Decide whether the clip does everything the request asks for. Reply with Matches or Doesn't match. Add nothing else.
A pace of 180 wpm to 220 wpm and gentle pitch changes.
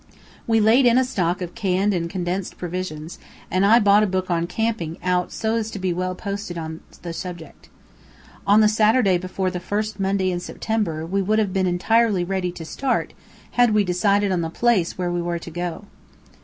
Doesn't match